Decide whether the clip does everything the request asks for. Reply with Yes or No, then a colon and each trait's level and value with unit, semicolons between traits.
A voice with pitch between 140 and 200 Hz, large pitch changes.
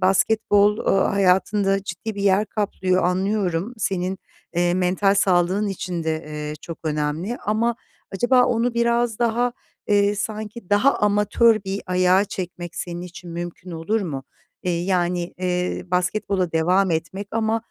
No: high, 190 Hz; average, 3.0 semitones